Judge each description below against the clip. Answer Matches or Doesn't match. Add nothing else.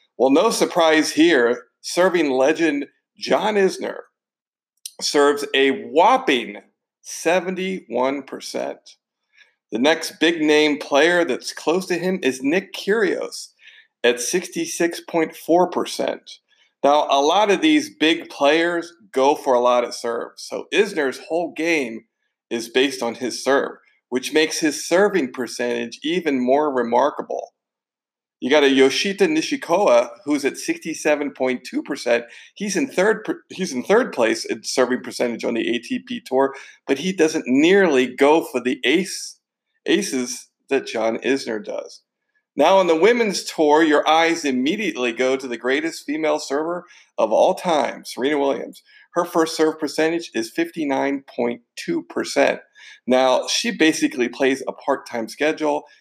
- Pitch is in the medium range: Matches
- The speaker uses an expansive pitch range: Matches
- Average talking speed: Doesn't match